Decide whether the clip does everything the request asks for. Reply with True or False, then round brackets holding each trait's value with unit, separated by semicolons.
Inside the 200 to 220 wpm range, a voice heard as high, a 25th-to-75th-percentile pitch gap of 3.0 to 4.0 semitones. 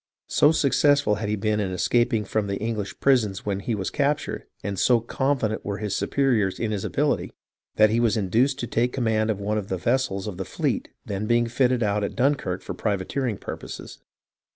False (205 wpm; 110 Hz; 3.5 semitones)